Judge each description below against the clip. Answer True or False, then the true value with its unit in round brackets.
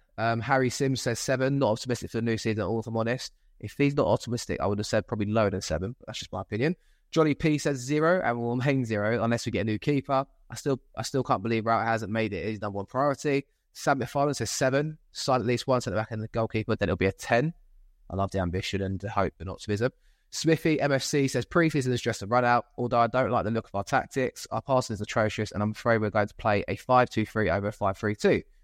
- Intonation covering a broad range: False (4.0 semitones)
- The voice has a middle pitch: False (115 Hz)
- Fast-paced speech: True (255 wpm)